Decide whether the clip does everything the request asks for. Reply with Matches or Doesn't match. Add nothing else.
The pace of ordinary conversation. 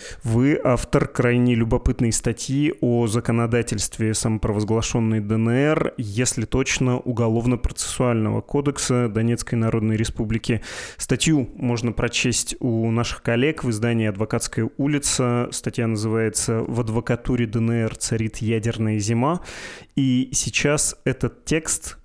Doesn't match